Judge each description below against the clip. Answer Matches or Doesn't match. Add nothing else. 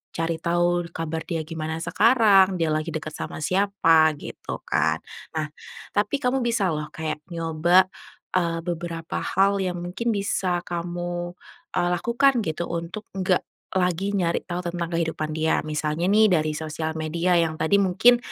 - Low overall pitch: Doesn't match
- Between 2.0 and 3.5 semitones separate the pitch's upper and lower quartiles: Matches